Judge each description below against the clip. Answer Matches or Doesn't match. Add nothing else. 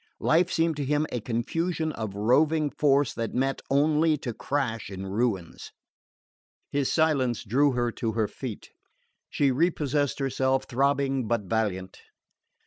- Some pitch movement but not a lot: Matches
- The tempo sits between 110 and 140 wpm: Matches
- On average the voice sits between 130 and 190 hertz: Matches